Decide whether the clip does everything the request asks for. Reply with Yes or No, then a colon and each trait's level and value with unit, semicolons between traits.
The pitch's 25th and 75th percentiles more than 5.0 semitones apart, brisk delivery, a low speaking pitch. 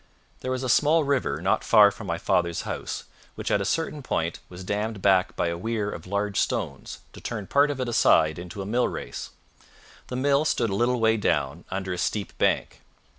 Yes: wide, 5.4 semitones; fast, 210 wpm; low, 105 Hz